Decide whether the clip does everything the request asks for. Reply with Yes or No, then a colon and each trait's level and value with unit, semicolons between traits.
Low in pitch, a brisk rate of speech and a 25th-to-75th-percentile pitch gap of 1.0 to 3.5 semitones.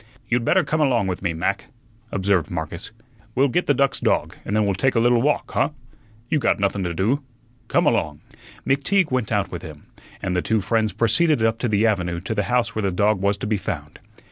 No: low, 105 Hz; fast, 220 wpm; average, 4.7 semitones